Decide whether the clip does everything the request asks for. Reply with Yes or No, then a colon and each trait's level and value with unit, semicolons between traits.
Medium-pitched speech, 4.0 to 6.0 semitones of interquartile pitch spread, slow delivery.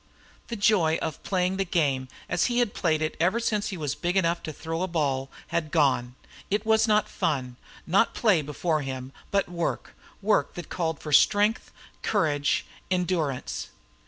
No: medium, 170 Hz; average, 4.8 semitones; average, 170 wpm